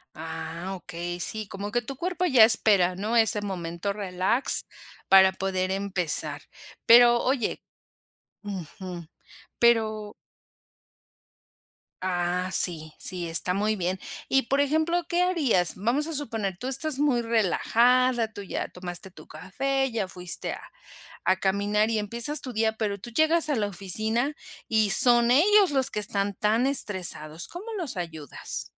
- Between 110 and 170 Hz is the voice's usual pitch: No, high, 210 Hz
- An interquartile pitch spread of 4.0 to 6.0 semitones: Yes, average, 5.2 semitones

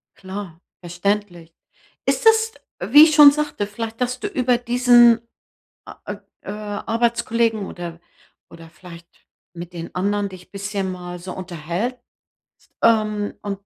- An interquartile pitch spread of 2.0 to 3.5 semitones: No, average, 5.0 semitones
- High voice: Yes, high, 205 Hz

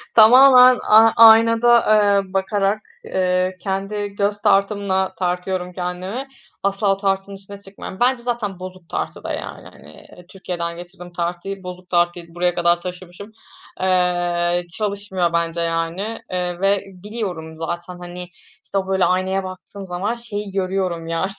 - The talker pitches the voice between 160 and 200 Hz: Yes, high, 190 Hz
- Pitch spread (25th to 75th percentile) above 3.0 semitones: No, narrow, 2.4 semitones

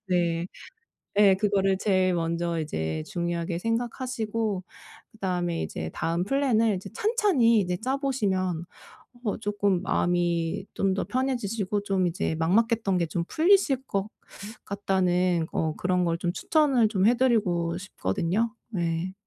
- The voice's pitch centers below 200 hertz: Yes, high, 190 Hz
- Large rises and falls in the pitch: No, average, 4.7 semitones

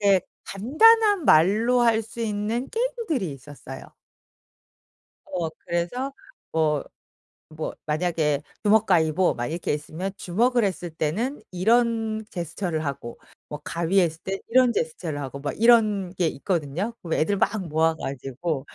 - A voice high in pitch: No, medium, 180 Hz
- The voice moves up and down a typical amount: No, wide, 6.3 semitones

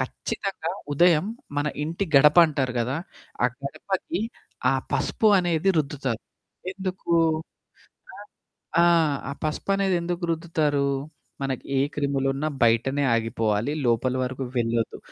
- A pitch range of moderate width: Yes, average, 4.6 semitones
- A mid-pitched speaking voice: Yes, medium, 145 Hz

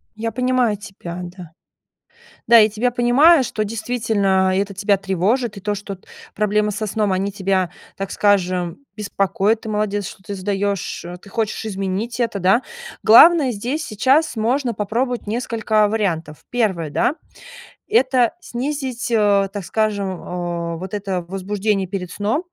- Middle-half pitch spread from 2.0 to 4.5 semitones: Yes, average, 3.3 semitones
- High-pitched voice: Yes, high, 210 Hz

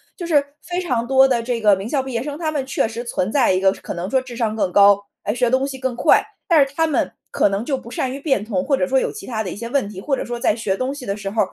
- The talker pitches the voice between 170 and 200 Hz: No, high, 240 Hz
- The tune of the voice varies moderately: Yes, average, 4.6 semitones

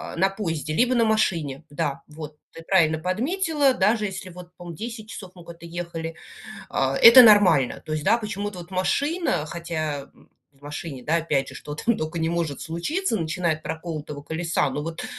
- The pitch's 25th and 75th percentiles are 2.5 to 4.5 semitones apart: No, average, 5.0 semitones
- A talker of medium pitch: Yes, medium, 170 Hz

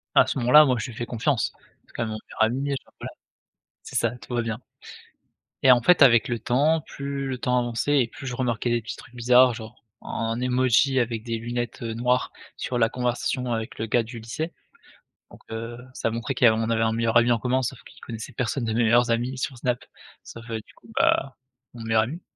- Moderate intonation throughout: No, narrow, 1.9 semitones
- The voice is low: Yes, low, 120 Hz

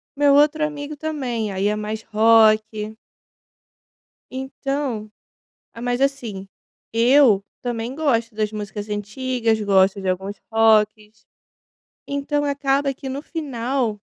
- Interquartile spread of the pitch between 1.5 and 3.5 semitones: No, average, 4.5 semitones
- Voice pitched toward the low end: No, high, 230 Hz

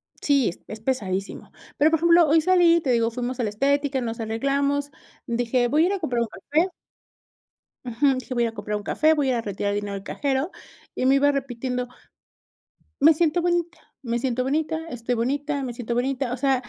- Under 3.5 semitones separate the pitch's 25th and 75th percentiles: No, average, 3.9 semitones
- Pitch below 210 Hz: No, very high, 265 Hz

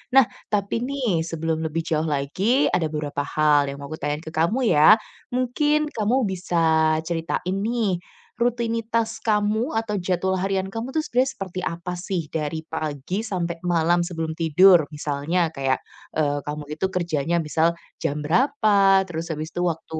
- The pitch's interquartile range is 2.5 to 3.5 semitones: No, average, 5.2 semitones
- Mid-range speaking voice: Yes, medium, 175 Hz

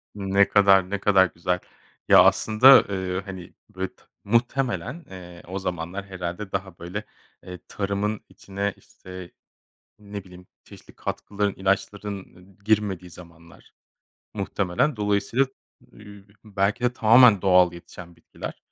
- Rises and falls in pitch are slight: Yes, narrow, 2.2 semitones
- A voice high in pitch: No, very low, 95 Hz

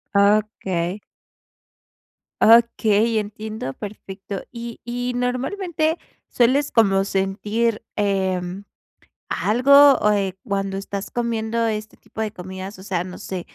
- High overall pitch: Yes, high, 210 Hz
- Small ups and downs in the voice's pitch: No, average, 3.3 semitones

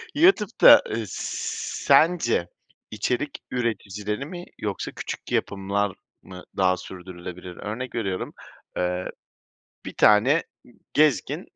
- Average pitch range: No, wide, 5.7 semitones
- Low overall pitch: Yes, low, 105 Hz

